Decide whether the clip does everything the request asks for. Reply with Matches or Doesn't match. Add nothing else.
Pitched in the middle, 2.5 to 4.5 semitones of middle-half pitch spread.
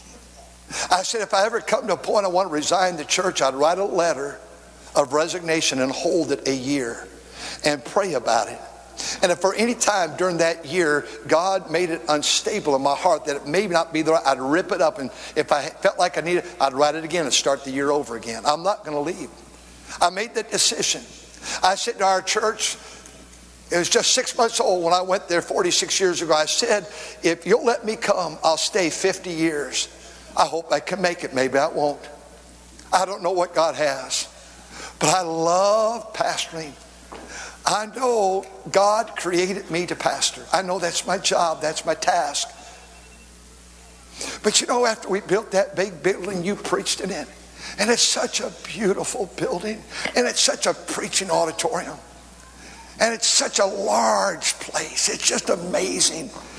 Doesn't match